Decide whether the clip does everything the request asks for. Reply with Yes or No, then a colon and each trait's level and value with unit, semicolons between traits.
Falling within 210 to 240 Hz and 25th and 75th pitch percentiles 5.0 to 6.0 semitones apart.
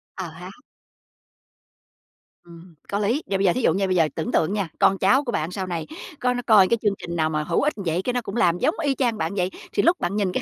No: high, 190 Hz; average, 5.3 semitones